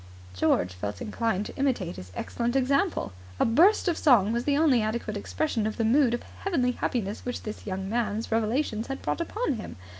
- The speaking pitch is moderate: No, high, 235 Hz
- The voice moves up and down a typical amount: Yes, average, 4.4 semitones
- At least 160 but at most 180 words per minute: No, average, 190 wpm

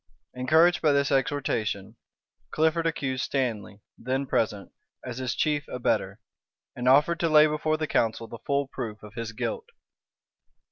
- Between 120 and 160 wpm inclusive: Yes, average, 145 wpm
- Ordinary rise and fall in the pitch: Yes, average, 4.9 semitones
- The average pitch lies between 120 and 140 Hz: Yes, low, 135 Hz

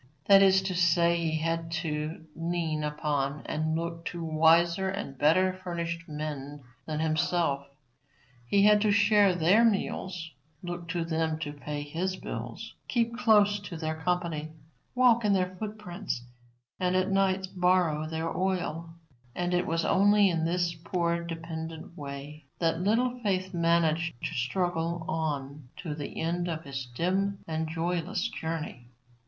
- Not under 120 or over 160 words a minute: Yes, average, 150 wpm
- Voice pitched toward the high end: No, medium, 170 Hz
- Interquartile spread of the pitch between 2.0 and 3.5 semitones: Yes, average, 2.8 semitones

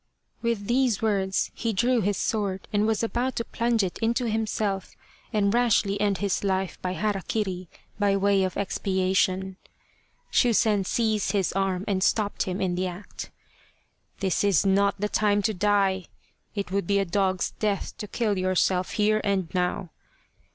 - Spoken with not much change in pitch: Yes, narrow, 2.1 semitones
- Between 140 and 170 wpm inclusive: Yes, average, 165 wpm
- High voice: Yes, high, 200 Hz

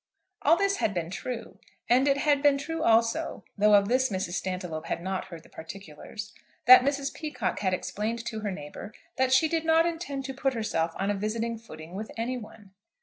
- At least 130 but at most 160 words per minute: No, fast, 205 wpm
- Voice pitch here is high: Yes, high, 225 Hz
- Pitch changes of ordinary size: No, wide, 6.2 semitones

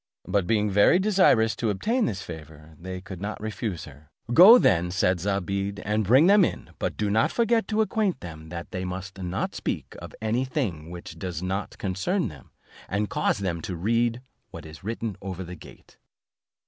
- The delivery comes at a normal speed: Yes, average, 185 wpm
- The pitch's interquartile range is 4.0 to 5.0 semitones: Yes, average, 4.6 semitones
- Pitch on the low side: Yes, low, 100 Hz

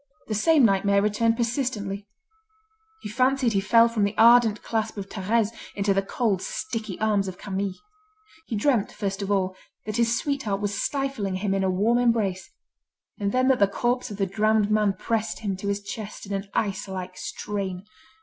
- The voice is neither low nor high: No, high, 210 Hz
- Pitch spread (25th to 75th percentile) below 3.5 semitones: Yes, average, 2.8 semitones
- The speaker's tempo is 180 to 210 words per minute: Yes, average, 185 wpm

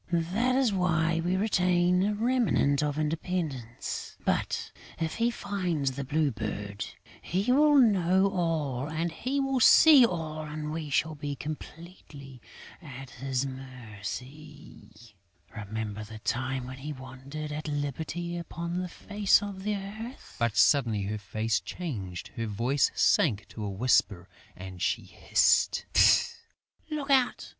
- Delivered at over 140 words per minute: No, slow, 135 wpm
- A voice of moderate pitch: Yes, medium, 150 Hz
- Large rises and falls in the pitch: Yes, wide, 6.4 semitones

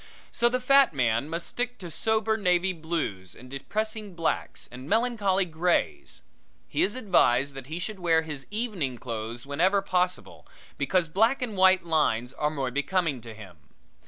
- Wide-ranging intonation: Yes, wide, 7.1 semitones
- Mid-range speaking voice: Yes, medium, 175 Hz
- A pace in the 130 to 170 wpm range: Yes, average, 160 wpm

